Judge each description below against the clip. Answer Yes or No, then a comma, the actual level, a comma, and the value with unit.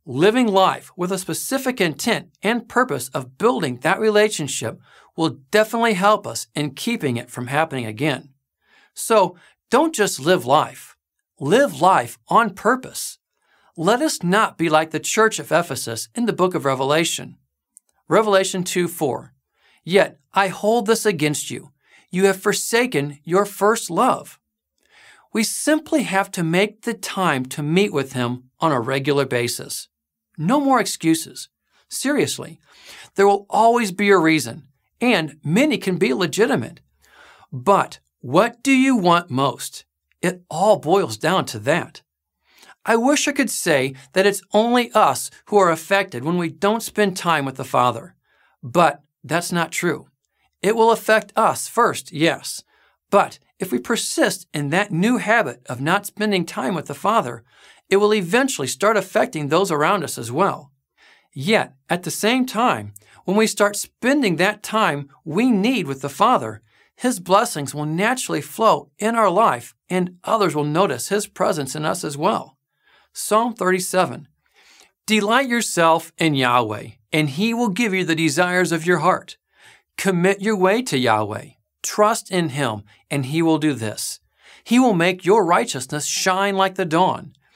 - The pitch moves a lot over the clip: Yes, wide, 6.4 semitones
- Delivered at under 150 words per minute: No, average, 155 wpm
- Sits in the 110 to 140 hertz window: No, medium, 185 Hz